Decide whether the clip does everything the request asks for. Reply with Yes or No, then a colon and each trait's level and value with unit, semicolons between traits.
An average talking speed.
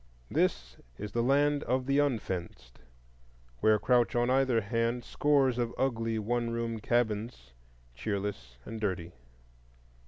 No: slow, 125 wpm